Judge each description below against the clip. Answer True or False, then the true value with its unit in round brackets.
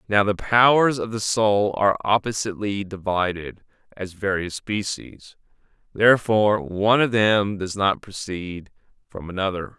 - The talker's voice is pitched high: False (100 Hz)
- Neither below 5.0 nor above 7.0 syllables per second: False (4.5 syllables/s)